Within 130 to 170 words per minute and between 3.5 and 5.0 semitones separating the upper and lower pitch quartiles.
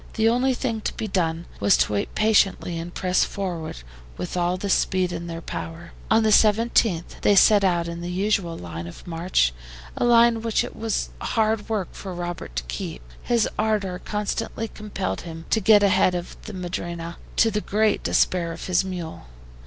No: average, 185 wpm; average, 4.1 semitones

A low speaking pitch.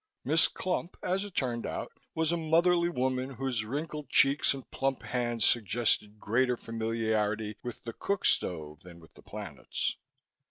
Yes: low, 125 Hz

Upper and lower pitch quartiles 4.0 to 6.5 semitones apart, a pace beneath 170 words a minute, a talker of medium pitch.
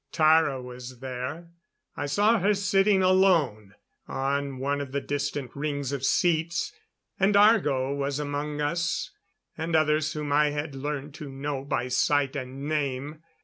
No: average, 2.8 semitones; average, 145 wpm; medium, 145 Hz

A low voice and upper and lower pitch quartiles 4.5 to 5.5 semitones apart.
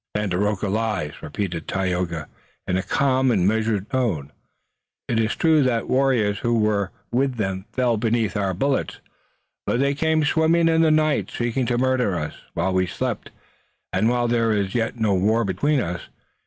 Yes: low, 110 Hz; average, 5.2 semitones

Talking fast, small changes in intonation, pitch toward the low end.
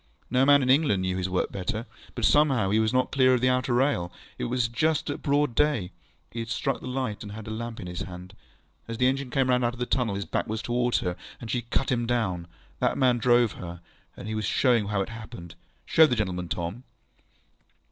No: fast, 230 wpm; average, 4.2 semitones; low, 120 Hz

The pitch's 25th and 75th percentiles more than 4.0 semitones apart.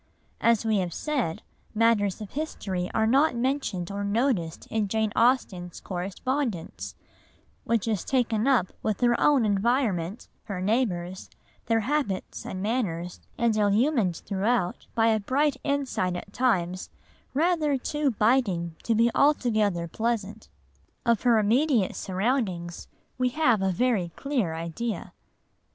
Yes: average, 5.1 semitones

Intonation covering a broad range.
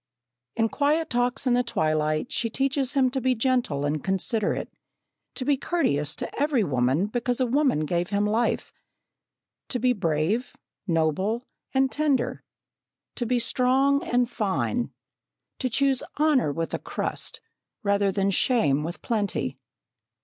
Yes: wide, 6.0 semitones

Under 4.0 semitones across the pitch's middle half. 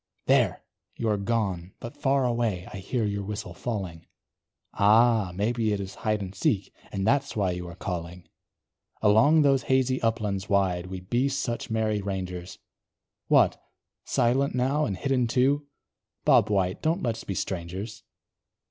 No: average, 4.3 semitones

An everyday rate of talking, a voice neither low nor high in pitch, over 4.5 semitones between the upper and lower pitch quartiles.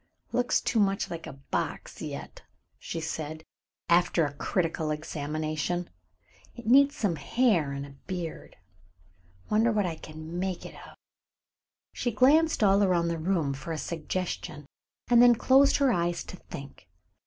Yes: average, 150 wpm; medium, 175 Hz; wide, 5.5 semitones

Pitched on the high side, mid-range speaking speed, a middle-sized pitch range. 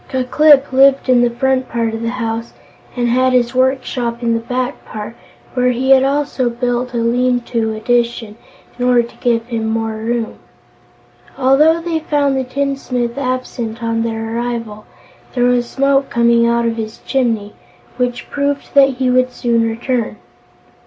No: high, 245 Hz; average, 170 wpm; narrow, 2.1 semitones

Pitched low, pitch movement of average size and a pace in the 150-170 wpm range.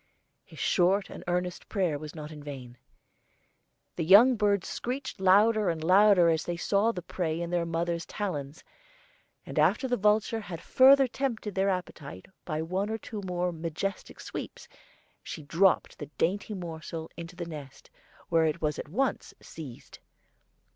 No: medium, 180 Hz; average, 4.3 semitones; average, 160 wpm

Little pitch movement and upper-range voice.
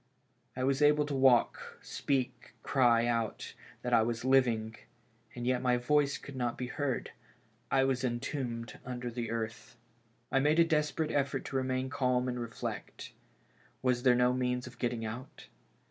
No: narrow, 2.0 semitones; low, 125 Hz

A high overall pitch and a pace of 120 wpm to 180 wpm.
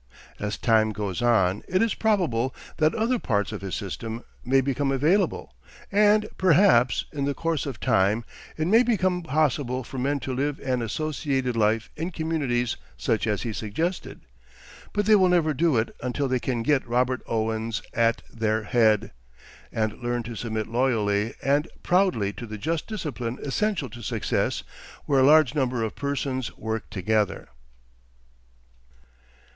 No: low, 130 Hz; average, 155 wpm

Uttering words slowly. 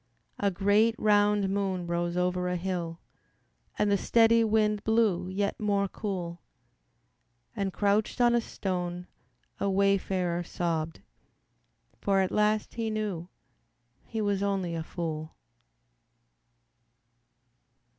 Yes: slow, 115 wpm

